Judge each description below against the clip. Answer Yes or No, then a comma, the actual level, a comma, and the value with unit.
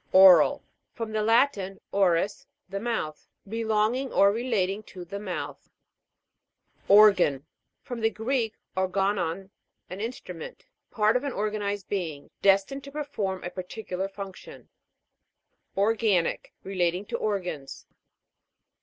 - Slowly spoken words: Yes, slow, 115 wpm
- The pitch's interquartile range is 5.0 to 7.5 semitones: No, average, 3.1 semitones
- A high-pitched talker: Yes, high, 200 Hz